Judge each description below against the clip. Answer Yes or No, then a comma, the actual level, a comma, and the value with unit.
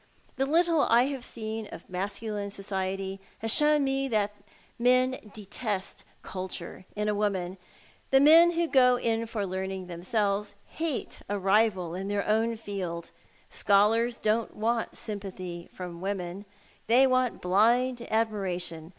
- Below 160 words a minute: Yes, average, 140 wpm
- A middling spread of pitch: Yes, average, 3.9 semitones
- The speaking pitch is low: No, high, 210 Hz